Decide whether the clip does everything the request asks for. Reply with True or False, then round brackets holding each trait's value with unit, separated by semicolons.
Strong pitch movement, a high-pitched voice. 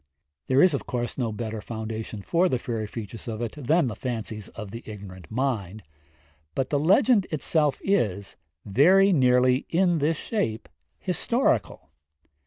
False (6.1 semitones; 125 Hz)